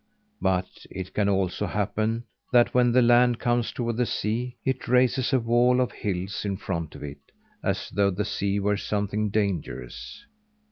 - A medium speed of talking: Yes, average, 170 wpm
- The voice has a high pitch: No, low, 105 Hz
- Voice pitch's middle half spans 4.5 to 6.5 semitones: No, average, 3.6 semitones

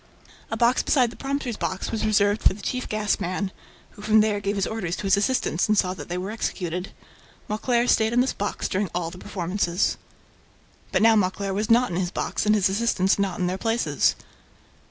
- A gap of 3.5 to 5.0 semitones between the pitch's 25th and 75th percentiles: No, average, 3.1 semitones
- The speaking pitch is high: Yes, high, 205 Hz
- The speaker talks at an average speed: No, fast, 210 wpm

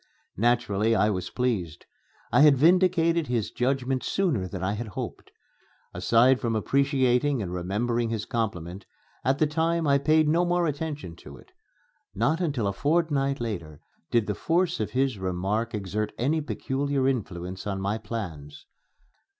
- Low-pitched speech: Yes, low, 120 Hz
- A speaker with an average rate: Yes, average, 150 wpm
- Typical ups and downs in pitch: No, wide, 6.4 semitones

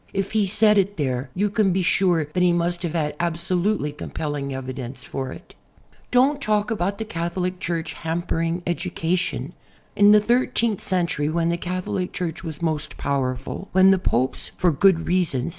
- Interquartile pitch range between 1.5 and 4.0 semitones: Yes, average, 3.7 semitones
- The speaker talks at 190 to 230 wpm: No, average, 175 wpm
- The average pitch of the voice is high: No, medium, 175 Hz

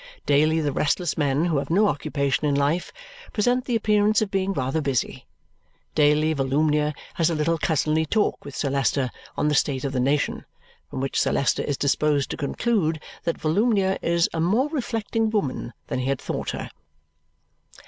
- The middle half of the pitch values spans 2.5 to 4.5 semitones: No, wide, 5.5 semitones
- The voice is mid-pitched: Yes, medium, 155 Hz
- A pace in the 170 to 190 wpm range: Yes, average, 180 wpm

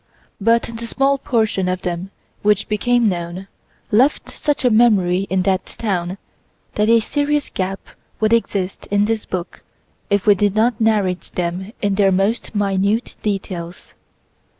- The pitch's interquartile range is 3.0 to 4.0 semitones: Yes, average, 3.3 semitones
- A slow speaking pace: No, average, 150 wpm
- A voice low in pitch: No, high, 205 Hz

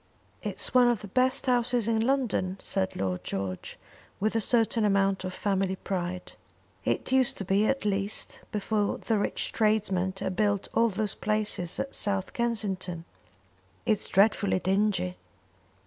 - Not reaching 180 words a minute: Yes, average, 145 wpm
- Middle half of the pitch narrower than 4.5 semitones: Yes, average, 3.0 semitones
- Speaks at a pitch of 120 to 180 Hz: No, high, 205 Hz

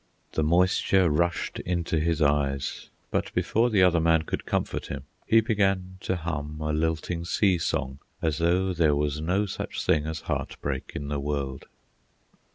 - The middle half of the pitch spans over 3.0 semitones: Yes, average, 3.6 semitones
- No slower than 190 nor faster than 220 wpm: No, average, 165 wpm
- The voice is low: Yes, very low, 80 Hz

